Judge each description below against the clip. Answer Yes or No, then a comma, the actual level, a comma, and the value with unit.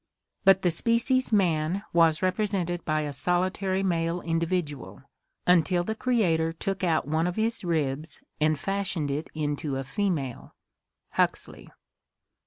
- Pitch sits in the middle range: Yes, medium, 175 Hz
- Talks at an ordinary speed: No, slow, 130 wpm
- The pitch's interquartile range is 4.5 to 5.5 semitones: No, average, 3.7 semitones